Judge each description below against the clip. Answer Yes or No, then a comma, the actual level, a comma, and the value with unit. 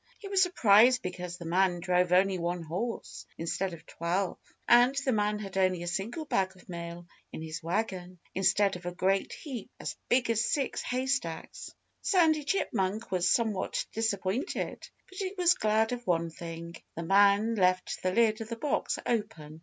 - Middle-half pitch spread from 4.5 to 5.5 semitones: Yes, average, 4.8 semitones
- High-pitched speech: Yes, high, 195 Hz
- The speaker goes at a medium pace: Yes, average, 175 wpm